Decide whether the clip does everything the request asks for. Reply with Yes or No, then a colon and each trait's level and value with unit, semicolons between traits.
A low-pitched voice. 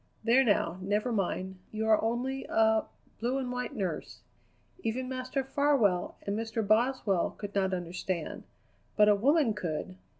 No: high, 220 Hz